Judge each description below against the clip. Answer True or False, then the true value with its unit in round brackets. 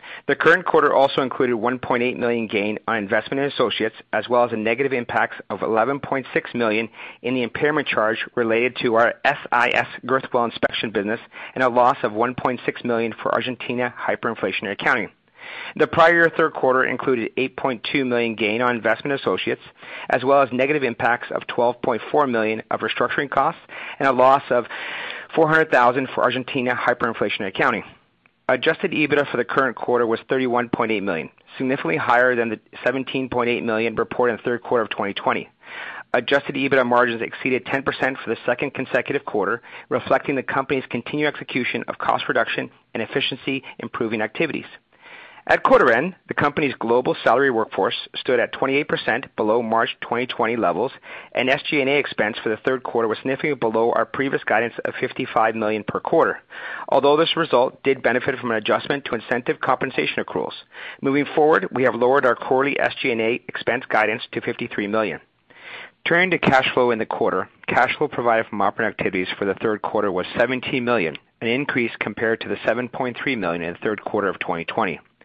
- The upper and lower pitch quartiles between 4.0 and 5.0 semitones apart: False (3.2 semitones)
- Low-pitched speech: True (125 Hz)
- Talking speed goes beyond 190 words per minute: False (175 wpm)